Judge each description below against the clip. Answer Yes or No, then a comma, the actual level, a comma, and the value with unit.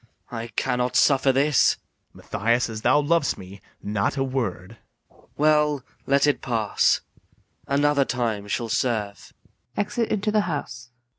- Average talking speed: No, slow, 120 wpm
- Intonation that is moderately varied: Yes, average, 4.5 semitones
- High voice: No, low, 125 Hz